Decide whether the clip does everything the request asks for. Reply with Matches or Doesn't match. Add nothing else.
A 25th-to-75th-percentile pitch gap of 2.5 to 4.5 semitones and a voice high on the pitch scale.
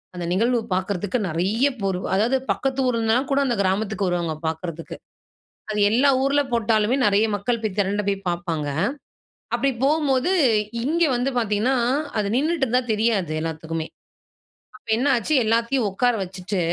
Doesn't match